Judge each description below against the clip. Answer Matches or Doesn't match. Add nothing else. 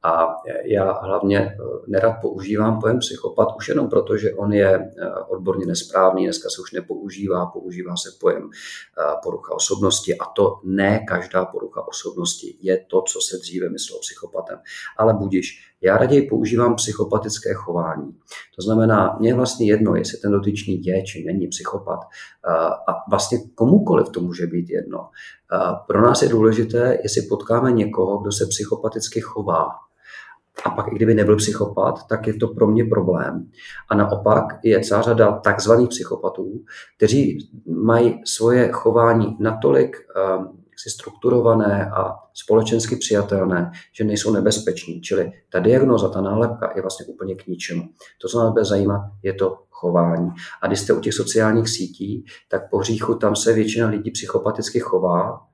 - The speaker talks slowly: Doesn't match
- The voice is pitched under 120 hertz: Matches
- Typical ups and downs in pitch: Matches